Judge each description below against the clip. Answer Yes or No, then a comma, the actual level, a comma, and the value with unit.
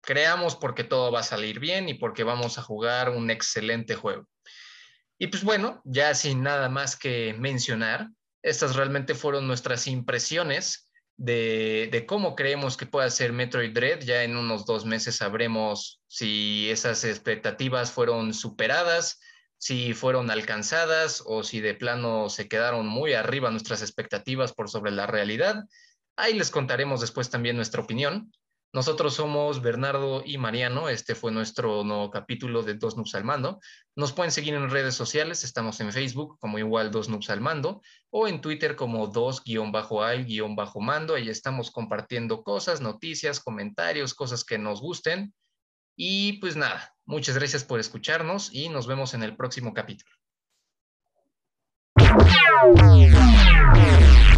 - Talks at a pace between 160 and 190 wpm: No, average, 150 wpm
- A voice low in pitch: Yes, low, 125 Hz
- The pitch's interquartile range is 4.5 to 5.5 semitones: Yes, average, 4.9 semitones